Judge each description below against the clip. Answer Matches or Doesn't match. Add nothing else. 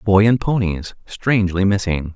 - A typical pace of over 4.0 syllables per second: Matches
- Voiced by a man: Matches